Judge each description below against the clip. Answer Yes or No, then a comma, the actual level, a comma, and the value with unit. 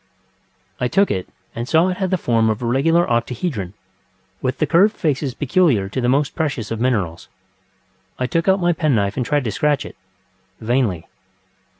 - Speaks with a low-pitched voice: Yes, low, 130 Hz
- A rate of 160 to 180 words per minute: Yes, average, 175 wpm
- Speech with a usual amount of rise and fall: No, wide, 6.2 semitones